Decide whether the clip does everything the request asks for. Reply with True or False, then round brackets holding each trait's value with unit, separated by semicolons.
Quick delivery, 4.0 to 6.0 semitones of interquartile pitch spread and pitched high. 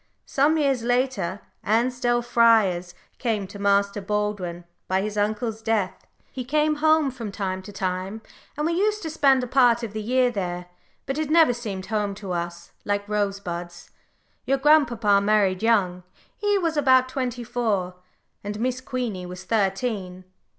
False (155 wpm; 4.7 semitones; 220 Hz)